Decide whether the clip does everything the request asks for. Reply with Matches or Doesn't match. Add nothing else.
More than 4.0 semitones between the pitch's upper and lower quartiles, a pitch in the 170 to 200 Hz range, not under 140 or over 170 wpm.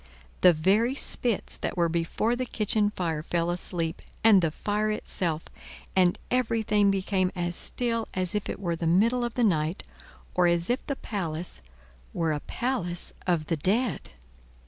Matches